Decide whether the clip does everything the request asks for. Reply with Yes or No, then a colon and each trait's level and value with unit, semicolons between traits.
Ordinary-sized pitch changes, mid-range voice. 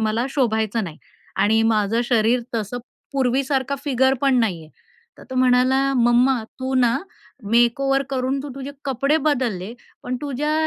No: average, 3.0 semitones; very high, 250 Hz